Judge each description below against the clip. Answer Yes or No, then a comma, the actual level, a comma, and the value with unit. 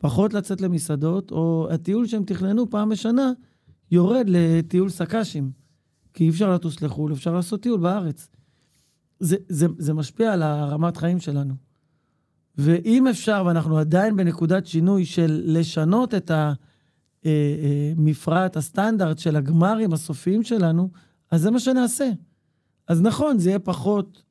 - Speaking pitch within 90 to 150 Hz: No, medium, 170 Hz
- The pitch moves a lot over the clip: No, average, 4.4 semitones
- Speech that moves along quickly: No, average, 130 wpm